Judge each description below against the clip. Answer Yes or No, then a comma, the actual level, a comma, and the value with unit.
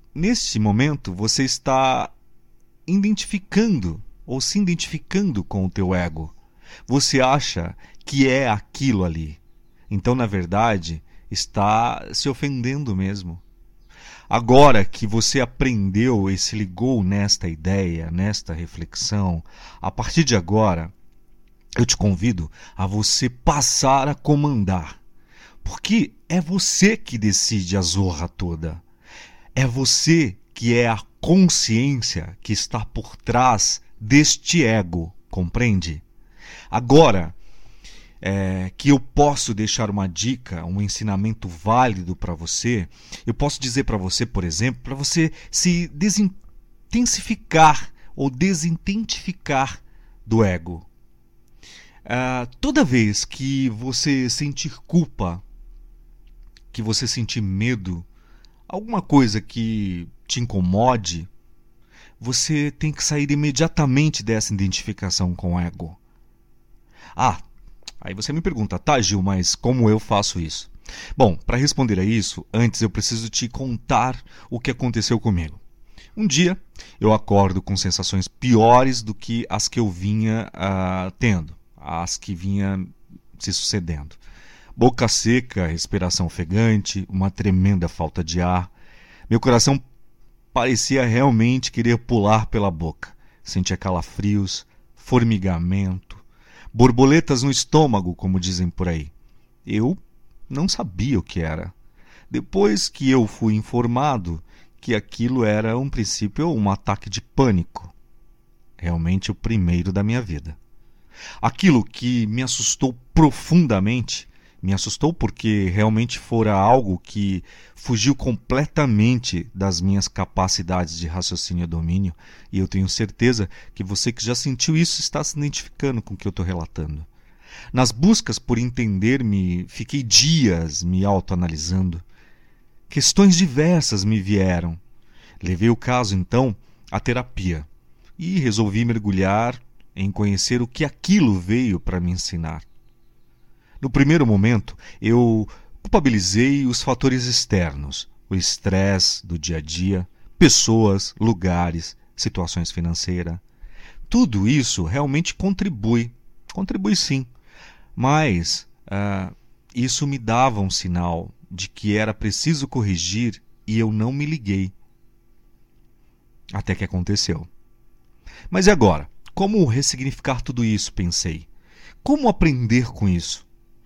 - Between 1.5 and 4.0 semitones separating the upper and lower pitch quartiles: No, wide, 5.6 semitones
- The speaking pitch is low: Yes, low, 110 Hz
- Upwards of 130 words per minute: No, slow, 120 wpm